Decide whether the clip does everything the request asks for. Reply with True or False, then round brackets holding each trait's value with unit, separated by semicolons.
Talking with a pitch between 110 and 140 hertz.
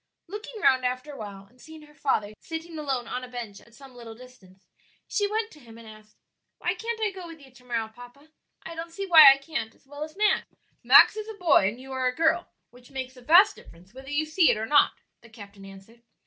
False (265 Hz)